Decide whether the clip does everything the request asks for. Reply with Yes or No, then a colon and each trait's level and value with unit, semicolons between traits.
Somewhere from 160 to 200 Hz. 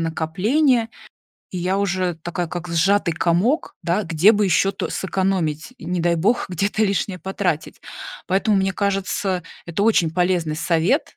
Yes: medium, 185 Hz